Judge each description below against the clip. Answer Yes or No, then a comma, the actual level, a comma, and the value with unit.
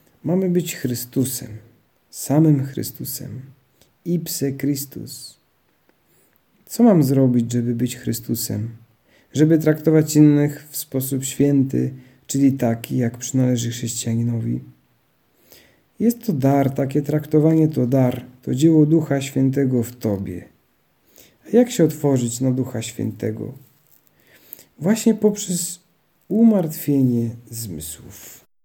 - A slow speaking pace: Yes, slow, 105 wpm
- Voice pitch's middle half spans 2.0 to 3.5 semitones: No, average, 4.4 semitones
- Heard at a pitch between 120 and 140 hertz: Yes, low, 135 Hz